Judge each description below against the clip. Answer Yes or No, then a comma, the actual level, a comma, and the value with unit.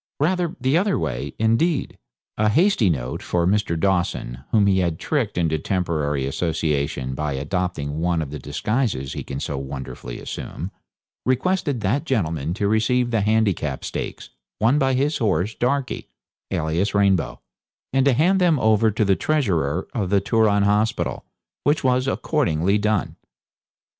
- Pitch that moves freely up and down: Yes, wide, 8.0 semitones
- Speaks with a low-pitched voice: Yes, low, 100 Hz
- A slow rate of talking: No, average, 150 wpm